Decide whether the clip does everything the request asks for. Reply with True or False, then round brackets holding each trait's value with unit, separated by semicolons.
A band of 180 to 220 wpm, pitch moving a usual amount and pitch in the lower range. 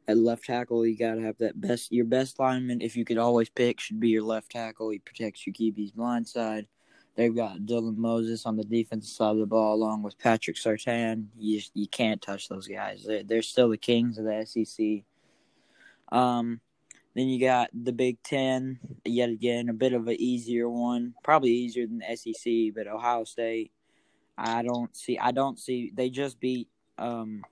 False (195 wpm; 1.6 semitones; 115 Hz)